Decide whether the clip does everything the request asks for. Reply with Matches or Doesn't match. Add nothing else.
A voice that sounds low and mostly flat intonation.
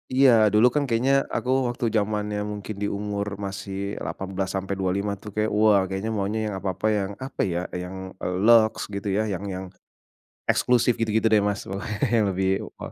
Matches